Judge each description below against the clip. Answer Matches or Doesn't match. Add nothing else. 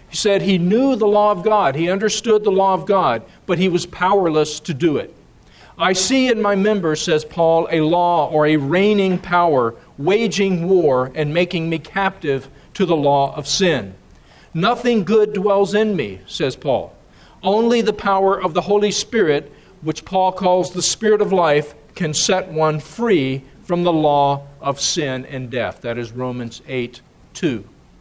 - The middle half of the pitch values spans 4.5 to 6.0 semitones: Matches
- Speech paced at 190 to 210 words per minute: Doesn't match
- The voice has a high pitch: Doesn't match